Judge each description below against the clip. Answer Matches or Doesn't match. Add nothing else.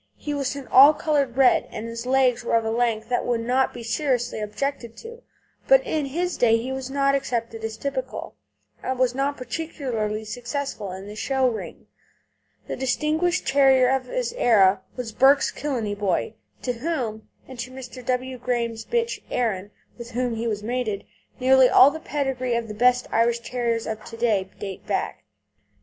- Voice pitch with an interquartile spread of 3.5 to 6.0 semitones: Doesn't match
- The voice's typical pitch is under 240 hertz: Doesn't match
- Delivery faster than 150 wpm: Matches